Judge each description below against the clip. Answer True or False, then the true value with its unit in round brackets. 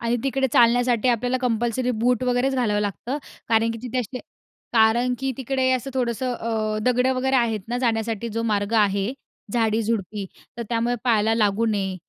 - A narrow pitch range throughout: True (2.3 semitones)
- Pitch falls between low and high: False (235 Hz)